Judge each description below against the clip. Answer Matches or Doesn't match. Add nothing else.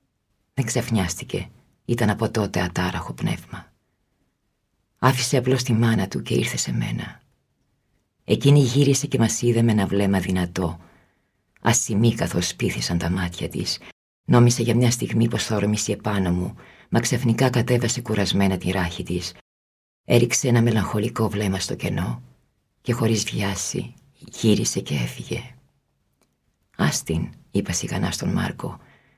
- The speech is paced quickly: Doesn't match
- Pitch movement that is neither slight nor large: Matches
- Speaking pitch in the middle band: Doesn't match